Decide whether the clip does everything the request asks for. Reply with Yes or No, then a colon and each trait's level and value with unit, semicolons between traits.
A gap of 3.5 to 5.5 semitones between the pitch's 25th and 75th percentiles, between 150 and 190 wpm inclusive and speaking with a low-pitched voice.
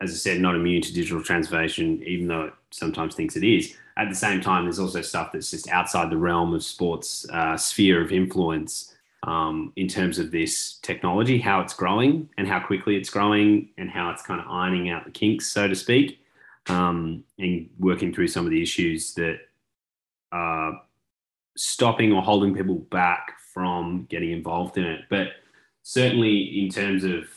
No: average, 3.1 semitones; average, 185 wpm; very low, 90 Hz